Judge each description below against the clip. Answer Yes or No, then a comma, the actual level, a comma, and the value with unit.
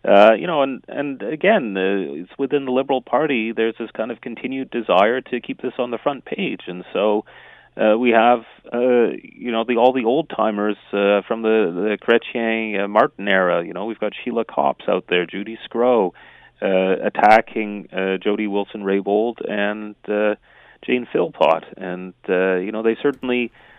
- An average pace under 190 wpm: Yes, average, 175 wpm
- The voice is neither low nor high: No, low, 110 Hz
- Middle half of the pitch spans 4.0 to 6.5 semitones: No, average, 3.0 semitones